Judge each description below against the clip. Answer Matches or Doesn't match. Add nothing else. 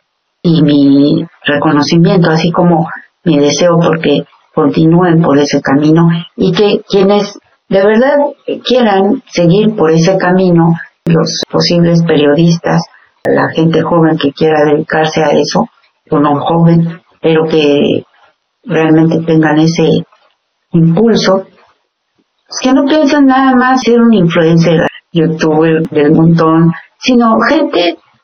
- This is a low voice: Doesn't match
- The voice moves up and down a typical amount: Matches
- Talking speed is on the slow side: Matches